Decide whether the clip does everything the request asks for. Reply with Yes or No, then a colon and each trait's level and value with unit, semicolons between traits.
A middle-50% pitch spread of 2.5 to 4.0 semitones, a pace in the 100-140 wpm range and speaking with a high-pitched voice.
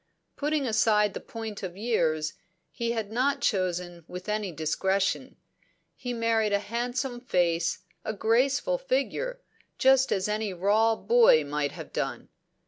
No: average, 5.0 semitones; slow, 135 wpm; high, 215 Hz